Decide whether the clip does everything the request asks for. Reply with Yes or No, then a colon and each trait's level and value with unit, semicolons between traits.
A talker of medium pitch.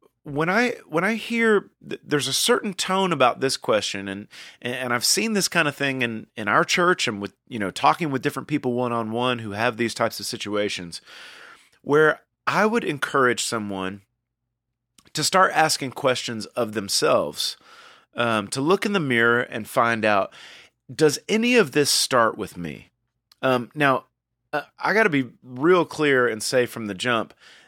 No: low, 125 Hz